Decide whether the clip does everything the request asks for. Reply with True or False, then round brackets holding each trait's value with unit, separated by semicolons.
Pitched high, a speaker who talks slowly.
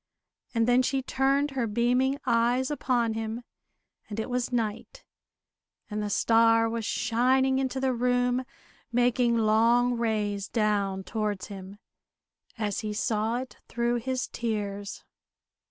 True (235 Hz; 130 wpm)